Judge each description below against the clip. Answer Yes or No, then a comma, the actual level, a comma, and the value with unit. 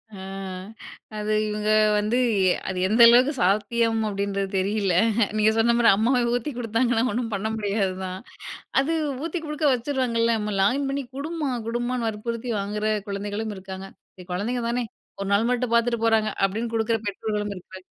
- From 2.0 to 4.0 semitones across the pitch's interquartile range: Yes, average, 3.0 semitones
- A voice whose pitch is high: Yes, high, 225 Hz